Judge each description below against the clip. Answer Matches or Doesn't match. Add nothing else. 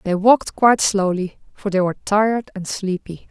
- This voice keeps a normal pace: Matches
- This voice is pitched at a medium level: Doesn't match